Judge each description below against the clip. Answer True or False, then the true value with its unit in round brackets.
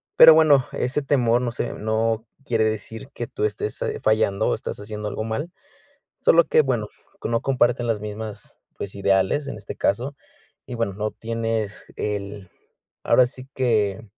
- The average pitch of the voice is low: True (115 Hz)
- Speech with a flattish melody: False (3.1 semitones)